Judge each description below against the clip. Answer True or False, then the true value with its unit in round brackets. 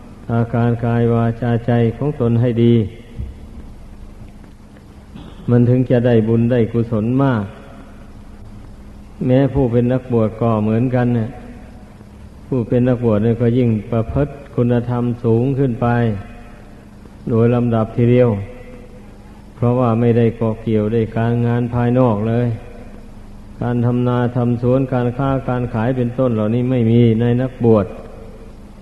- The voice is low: True (120 Hz)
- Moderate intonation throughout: False (1.6 semitones)